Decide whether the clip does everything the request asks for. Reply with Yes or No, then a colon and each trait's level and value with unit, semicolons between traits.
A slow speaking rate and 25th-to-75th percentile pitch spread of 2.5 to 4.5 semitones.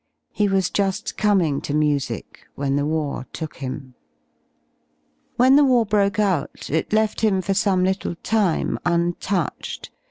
No: slow, 125 wpm; wide, 5.5 semitones